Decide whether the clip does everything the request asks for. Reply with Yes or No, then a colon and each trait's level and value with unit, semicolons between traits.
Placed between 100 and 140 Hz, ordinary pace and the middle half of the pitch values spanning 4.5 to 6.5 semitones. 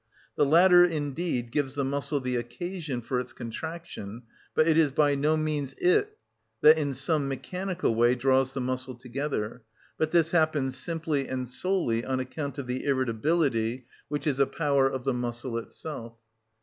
No: low, 135 Hz; average, 165 wpm; average, 3.8 semitones